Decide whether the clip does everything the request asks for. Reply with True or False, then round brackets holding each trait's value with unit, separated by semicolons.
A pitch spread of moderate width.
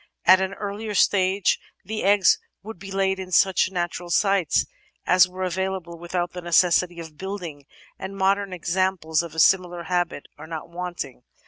False (1.9 semitones)